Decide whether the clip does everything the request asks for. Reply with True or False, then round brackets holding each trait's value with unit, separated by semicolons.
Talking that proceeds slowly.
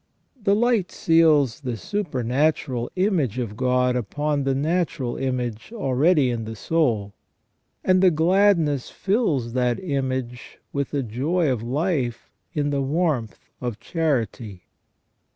True (125 wpm)